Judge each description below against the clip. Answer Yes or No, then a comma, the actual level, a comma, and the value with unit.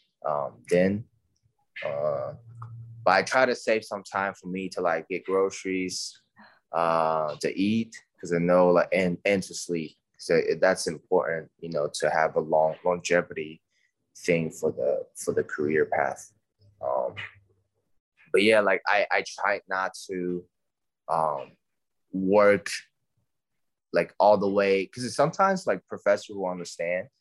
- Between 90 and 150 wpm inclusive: Yes, average, 145 wpm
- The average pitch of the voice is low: Yes, low, 100 Hz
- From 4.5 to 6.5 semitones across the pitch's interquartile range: Yes, average, 5.2 semitones